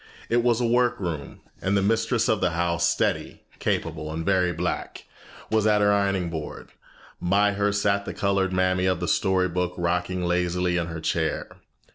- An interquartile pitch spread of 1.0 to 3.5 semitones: Yes, average, 2.8 semitones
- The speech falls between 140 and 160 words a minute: No, average, 175 wpm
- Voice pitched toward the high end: No, very low, 95 Hz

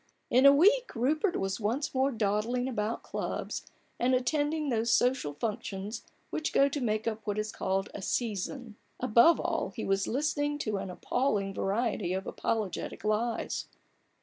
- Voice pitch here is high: Yes, high, 230 Hz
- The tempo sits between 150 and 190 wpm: Yes, average, 155 wpm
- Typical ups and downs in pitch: Yes, average, 4.6 semitones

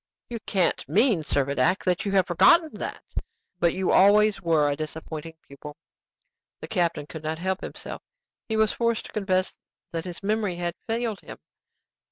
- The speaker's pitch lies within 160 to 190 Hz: Yes, medium, 185 Hz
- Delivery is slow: No, average, 165 wpm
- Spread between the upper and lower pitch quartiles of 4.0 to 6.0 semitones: Yes, average, 4.6 semitones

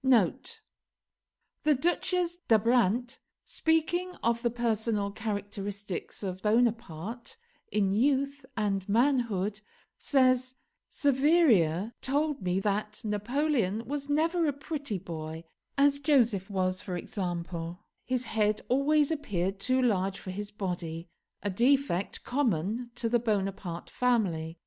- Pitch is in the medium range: No, high, 220 Hz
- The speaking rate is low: Yes, slow, 110 wpm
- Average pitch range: No, wide, 5.8 semitones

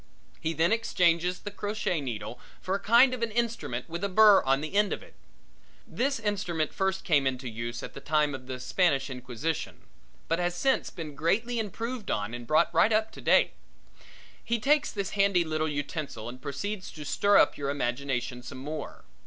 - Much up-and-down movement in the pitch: Yes, wide, 7.0 semitones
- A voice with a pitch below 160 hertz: No, medium, 170 Hz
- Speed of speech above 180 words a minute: Yes, average, 190 wpm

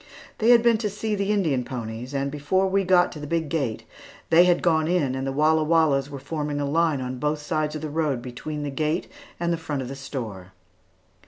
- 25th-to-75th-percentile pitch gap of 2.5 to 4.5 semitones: Yes, average, 3.7 semitones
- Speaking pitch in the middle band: Yes, medium, 150 Hz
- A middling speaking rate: No, fast, 230 wpm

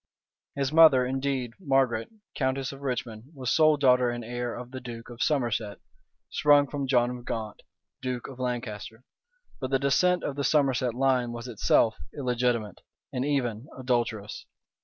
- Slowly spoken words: No, average, 155 wpm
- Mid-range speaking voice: No, low, 125 Hz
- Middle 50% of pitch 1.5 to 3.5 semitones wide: Yes, narrow, 2.4 semitones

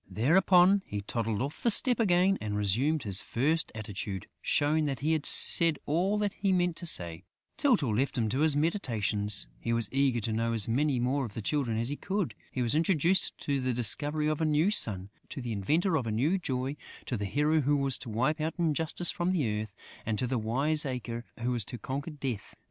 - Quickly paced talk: Yes, fast, 215 wpm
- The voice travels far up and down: Yes, wide, 5.8 semitones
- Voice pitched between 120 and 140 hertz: Yes, low, 135 Hz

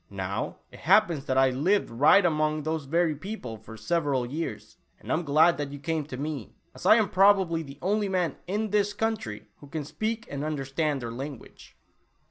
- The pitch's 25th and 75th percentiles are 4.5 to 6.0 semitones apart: Yes, average, 5.1 semitones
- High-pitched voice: No, medium, 155 Hz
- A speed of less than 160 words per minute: No, average, 185 wpm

